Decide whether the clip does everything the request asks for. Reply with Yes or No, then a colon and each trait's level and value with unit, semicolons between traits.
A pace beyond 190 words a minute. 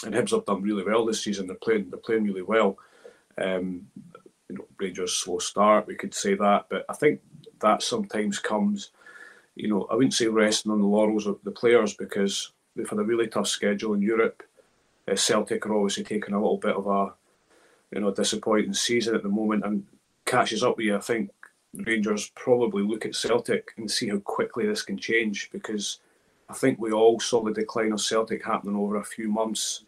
Yes: fast, 205 wpm